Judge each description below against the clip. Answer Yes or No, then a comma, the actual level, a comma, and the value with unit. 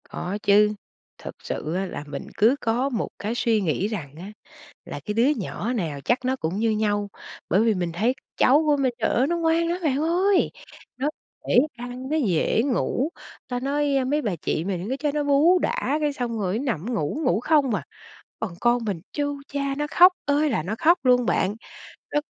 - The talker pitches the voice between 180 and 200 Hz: No, high, 245 Hz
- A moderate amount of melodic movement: No, wide, 5.7 semitones